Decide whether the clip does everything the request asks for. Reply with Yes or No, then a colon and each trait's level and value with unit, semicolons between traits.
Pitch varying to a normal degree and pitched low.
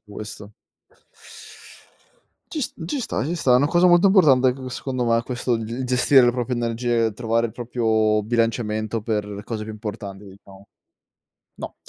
Yes: average, 3.0 semitones; low, 115 Hz